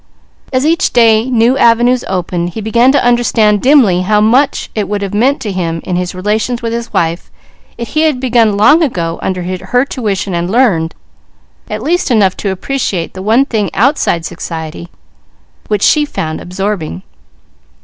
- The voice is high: Yes, high, 215 Hz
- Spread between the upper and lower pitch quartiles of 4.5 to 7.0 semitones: Yes, average, 5.2 semitones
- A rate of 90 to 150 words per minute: No, average, 170 wpm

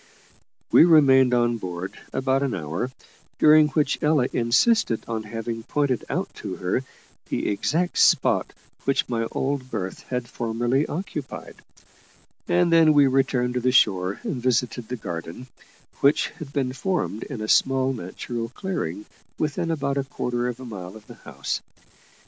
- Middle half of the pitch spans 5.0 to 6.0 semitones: No, average, 3.8 semitones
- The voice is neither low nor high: No, low, 125 Hz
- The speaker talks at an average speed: Yes, average, 155 wpm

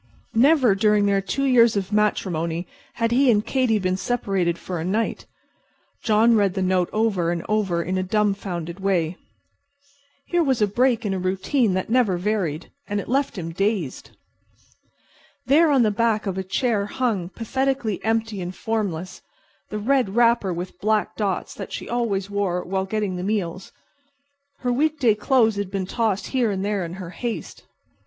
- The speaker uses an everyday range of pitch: Yes, average, 3.7 semitones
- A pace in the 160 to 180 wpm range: Yes, average, 175 wpm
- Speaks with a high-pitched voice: Yes, high, 205 Hz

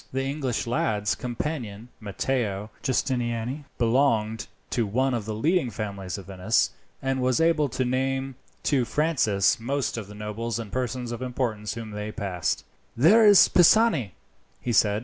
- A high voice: No, low, 120 Hz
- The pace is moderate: Yes, average, 150 wpm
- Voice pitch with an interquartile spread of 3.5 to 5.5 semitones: Yes, average, 4.0 semitones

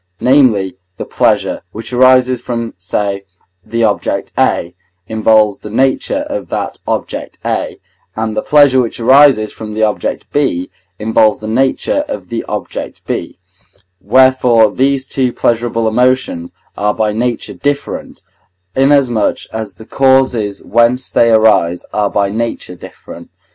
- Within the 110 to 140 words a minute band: Yes, slow, 135 wpm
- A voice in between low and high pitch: No, low, 115 Hz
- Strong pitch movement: No, average, 3.4 semitones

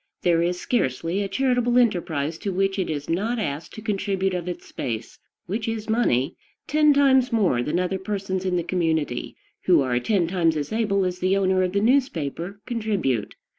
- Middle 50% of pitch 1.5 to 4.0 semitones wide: No, average, 4.8 semitones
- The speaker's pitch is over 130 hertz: Yes, high, 190 Hz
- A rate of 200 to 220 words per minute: No, average, 185 wpm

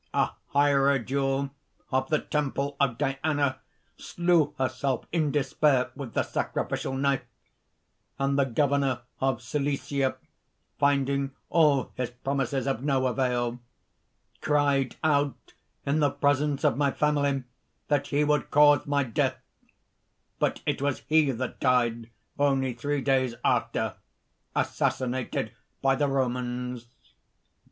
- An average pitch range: No, narrow, 1.7 semitones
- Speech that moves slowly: Yes, slow, 120 wpm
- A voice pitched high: No, medium, 140 Hz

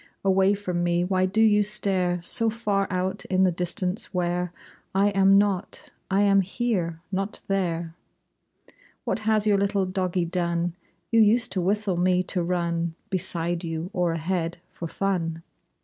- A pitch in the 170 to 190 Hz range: Yes, medium, 185 Hz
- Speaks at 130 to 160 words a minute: Yes, average, 155 wpm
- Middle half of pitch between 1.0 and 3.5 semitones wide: Yes, narrow, 2.4 semitones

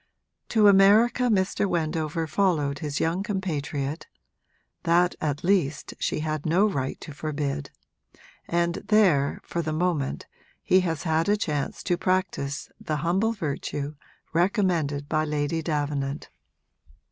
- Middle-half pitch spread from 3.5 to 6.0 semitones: Yes, average, 4.3 semitones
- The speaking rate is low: Yes, slow, 125 wpm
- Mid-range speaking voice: Yes, medium, 160 Hz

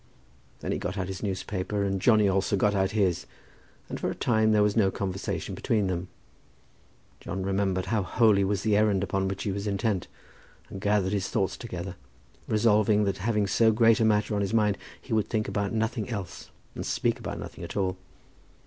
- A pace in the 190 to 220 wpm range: Yes, average, 195 wpm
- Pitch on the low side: Yes, low, 100 Hz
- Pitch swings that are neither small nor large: No, narrow, 2.0 semitones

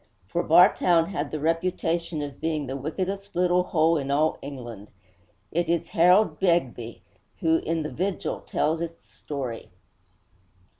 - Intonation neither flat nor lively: Yes, average, 3.4 semitones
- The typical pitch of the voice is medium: Yes, medium, 165 Hz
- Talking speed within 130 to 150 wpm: Yes, average, 140 wpm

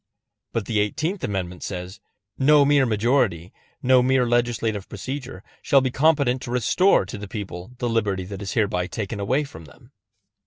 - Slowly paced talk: No, average, 165 wpm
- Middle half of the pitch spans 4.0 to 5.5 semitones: Yes, average, 5.1 semitones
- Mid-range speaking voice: No, low, 115 Hz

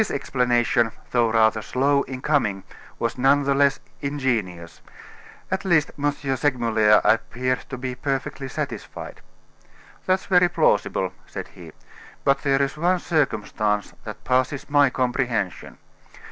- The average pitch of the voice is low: Yes, low, 130 Hz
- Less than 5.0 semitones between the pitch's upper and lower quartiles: Yes, average, 3.5 semitones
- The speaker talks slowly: Yes, slow, 130 wpm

